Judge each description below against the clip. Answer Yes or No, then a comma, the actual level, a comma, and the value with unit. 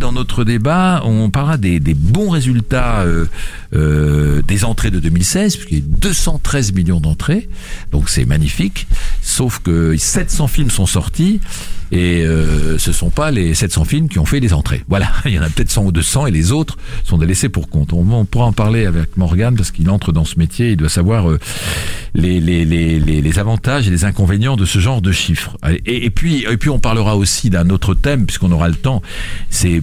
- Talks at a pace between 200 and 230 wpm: Yes, average, 210 wpm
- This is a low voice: Yes, very low, 95 Hz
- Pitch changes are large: Yes, wide, 6.2 semitones